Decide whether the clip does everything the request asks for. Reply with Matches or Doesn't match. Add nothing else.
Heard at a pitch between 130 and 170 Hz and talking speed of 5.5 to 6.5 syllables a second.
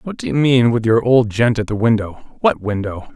Doesn't match